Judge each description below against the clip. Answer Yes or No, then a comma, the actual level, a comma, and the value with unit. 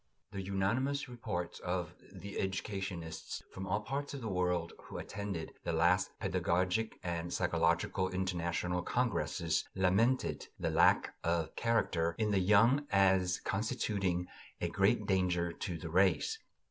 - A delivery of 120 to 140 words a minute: Yes, slow, 135 wpm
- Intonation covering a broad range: No, average, 3.1 semitones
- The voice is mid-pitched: No, very low, 95 Hz